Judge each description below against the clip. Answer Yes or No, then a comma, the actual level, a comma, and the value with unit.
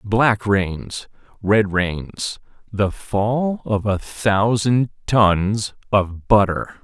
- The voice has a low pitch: Yes, low, 105 Hz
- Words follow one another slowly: Yes, slow, 90 wpm